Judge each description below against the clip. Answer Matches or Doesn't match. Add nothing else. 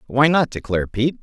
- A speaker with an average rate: Matches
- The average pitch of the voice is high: Doesn't match